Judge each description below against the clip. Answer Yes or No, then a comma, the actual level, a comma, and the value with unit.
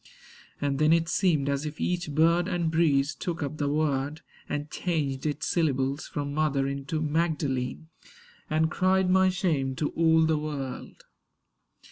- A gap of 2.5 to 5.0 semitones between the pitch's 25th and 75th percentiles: Yes, average, 2.9 semitones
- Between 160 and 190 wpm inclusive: No, average, 150 wpm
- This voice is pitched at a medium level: Yes, medium, 155 Hz